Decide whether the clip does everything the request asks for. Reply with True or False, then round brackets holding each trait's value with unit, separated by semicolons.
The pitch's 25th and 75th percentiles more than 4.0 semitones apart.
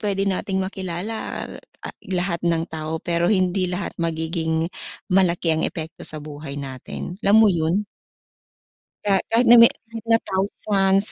False (3.5 semitones)